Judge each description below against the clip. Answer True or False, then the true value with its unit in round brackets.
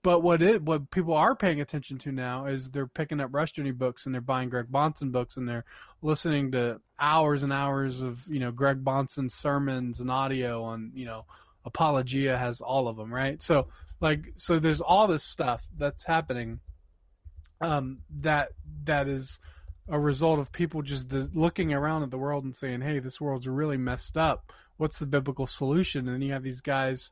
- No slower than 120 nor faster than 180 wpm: False (195 wpm)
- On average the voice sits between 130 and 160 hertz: True (135 Hz)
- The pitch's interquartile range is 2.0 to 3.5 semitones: True (3.1 semitones)